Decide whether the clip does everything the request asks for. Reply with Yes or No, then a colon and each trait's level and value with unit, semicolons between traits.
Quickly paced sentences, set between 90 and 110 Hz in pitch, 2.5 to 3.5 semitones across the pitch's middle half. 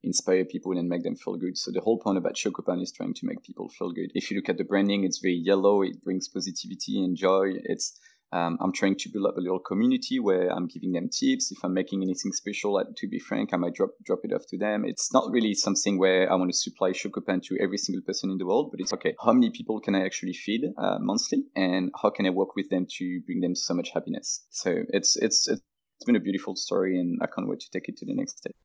No: fast, 265 wpm; very low, 95 Hz; average, 3.9 semitones